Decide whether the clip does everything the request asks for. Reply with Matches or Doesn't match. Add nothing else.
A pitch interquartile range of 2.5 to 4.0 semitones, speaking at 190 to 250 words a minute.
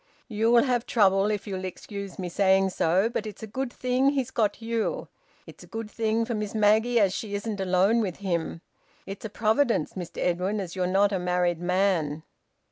Matches